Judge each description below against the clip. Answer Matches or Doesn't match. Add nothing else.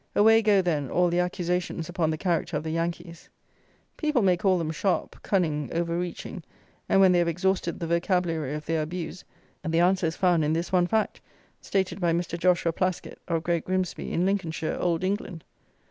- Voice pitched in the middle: Matches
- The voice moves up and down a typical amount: Doesn't match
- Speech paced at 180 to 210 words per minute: Matches